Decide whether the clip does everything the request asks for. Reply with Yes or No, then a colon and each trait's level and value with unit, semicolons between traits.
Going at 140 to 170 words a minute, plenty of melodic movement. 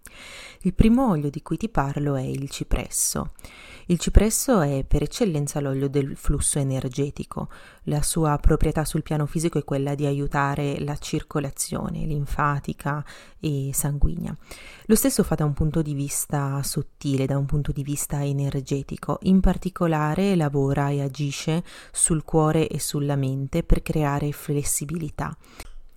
No: average, 145 wpm; narrow, 2.4 semitones